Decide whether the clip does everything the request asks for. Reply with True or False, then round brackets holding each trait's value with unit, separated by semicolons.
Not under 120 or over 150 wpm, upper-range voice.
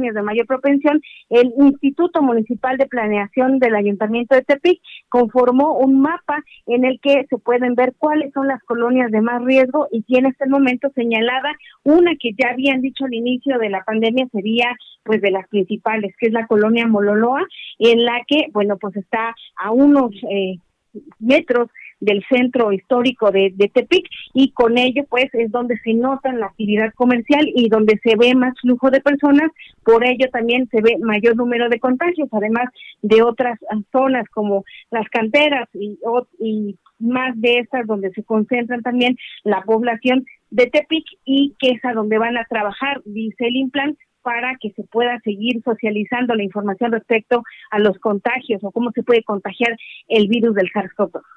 False (175 wpm; 240 Hz)